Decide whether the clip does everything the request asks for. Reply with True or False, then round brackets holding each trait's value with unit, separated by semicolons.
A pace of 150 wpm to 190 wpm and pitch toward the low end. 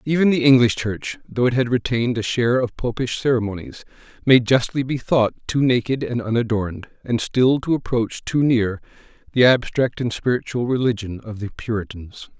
True (170 wpm; 120 Hz)